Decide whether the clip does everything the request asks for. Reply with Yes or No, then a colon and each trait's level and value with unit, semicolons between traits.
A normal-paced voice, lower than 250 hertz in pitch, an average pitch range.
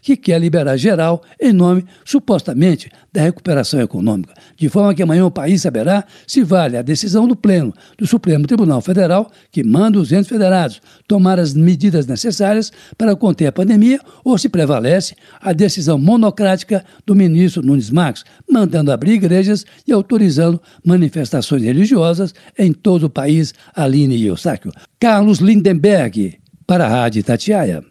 Yes: average, 150 wpm; medium, 185 Hz; average, 4.4 semitones